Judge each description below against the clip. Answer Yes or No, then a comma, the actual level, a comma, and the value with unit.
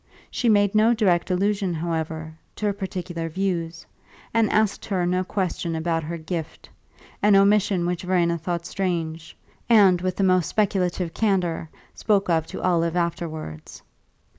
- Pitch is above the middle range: No, medium, 180 Hz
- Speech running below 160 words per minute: Yes, average, 145 wpm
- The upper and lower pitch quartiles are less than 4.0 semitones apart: Yes, average, 2.9 semitones